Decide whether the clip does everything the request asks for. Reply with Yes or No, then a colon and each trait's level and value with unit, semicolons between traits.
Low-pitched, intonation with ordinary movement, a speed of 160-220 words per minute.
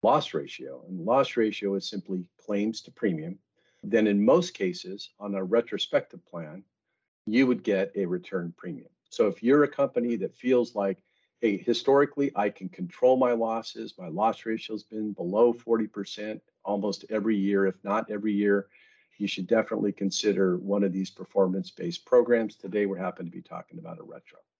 Yes: low, 105 Hz; average, 3.2 semitones; average, 175 wpm